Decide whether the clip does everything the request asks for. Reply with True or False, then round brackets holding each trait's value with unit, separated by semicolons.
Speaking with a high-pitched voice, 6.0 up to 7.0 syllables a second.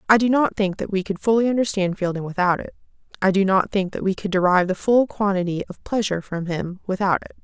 True (195 Hz; 6.2 syllables/s)